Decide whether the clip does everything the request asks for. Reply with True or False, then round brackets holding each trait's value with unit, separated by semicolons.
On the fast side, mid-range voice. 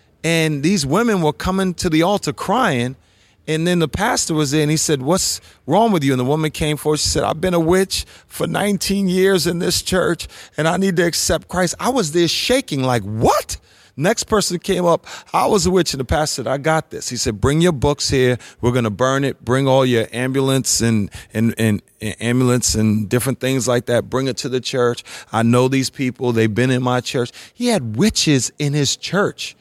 True (225 wpm; 145 Hz)